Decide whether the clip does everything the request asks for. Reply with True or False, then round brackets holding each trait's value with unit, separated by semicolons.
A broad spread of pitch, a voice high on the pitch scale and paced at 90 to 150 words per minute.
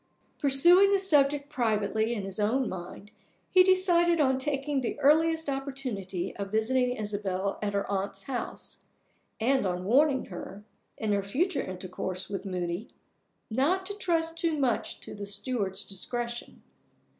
True (6.6 semitones; 240 Hz; 145 wpm)